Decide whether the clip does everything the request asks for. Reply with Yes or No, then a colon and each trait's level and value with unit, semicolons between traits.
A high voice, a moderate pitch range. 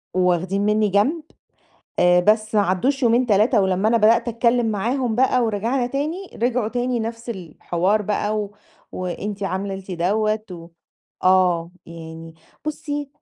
Yes: high, 210 Hz; average, 4.5 semitones